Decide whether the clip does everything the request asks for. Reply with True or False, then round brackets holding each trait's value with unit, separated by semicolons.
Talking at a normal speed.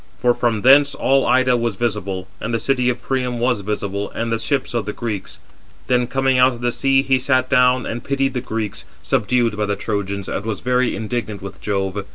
False (215 wpm)